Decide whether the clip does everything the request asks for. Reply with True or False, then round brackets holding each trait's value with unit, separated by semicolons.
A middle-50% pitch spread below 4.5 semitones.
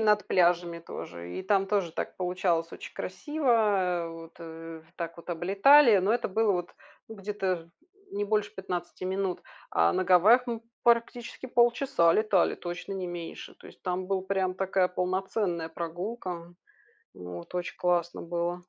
True (3.2 semitones)